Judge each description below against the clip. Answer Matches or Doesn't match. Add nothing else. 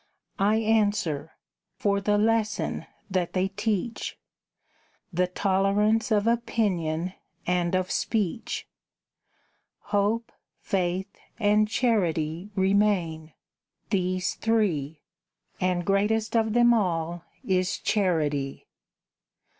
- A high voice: Matches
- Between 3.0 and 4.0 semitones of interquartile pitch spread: Matches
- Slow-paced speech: Matches